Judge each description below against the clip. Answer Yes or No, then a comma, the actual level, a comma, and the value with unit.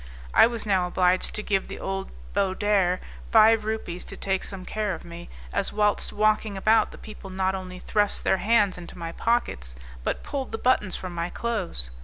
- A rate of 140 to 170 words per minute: No, average, 190 wpm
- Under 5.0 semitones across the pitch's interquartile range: Yes, average, 2.8 semitones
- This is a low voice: No, high, 195 Hz